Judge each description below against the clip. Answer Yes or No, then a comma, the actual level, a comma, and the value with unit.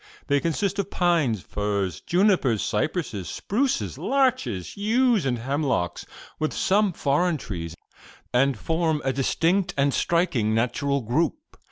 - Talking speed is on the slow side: Yes, slow, 125 wpm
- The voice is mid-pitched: Yes, medium, 150 Hz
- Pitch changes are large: Yes, wide, 7.5 semitones